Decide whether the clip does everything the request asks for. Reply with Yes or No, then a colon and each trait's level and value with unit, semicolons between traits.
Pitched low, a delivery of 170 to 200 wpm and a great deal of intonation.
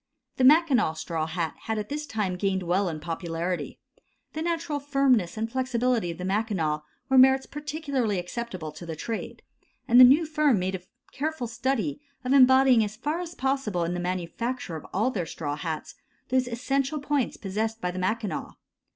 No: high, 225 Hz; average, 175 wpm; wide, 7.0 semitones